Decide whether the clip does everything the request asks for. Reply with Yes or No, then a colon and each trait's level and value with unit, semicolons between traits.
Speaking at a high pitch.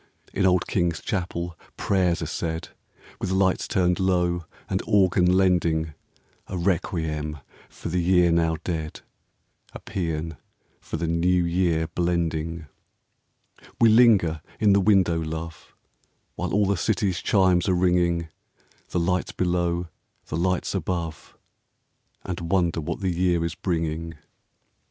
No: very low, 85 Hz